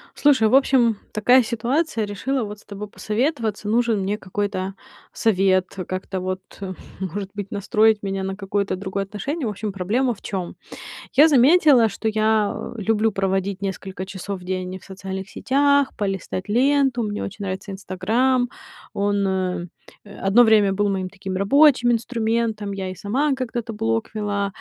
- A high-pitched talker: Yes, high, 205 Hz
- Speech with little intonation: No, average, 3.5 semitones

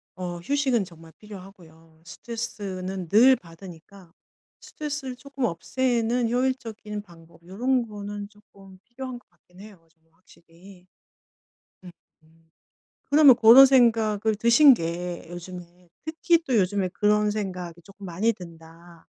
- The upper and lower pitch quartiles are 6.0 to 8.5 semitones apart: No, average, 5.2 semitones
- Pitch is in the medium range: No, high, 200 Hz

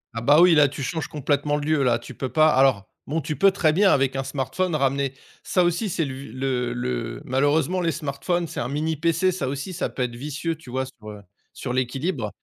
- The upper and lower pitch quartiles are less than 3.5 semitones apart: No, average, 3.8 semitones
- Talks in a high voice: No, medium, 140 Hz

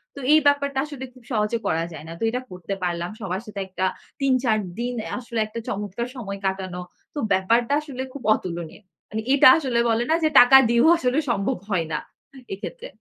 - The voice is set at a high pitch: Yes, high, 225 Hz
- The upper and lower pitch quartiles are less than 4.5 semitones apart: No, average, 5.1 semitones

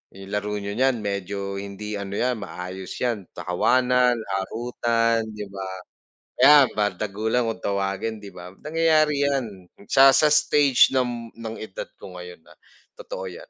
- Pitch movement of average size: Yes, average, 4.2 semitones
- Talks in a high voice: No, low, 110 Hz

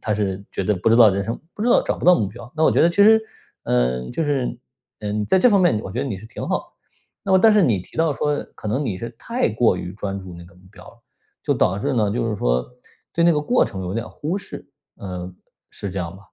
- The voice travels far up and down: Yes, wide, 7.9 semitones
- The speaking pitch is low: Yes, low, 110 Hz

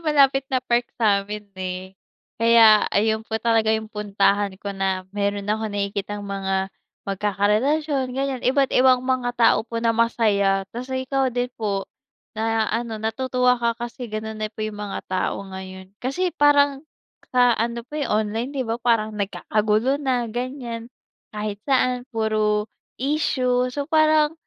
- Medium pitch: No, high, 225 Hz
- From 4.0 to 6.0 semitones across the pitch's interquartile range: No, average, 3.6 semitones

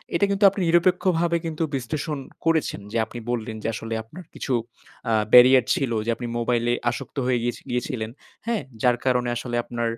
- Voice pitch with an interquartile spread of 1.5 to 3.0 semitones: No, wide, 5.5 semitones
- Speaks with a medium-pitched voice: No, low, 125 Hz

